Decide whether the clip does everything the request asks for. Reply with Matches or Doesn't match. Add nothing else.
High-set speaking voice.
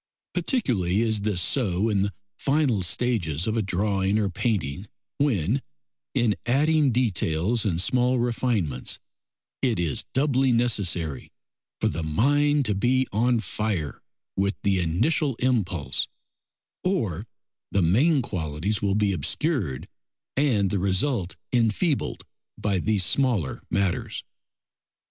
Doesn't match